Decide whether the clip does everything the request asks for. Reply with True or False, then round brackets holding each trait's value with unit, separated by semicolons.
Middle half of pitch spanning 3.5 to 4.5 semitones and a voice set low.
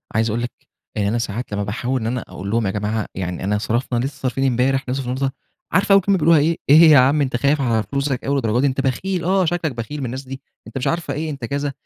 True (3.8 semitones; 130 Hz)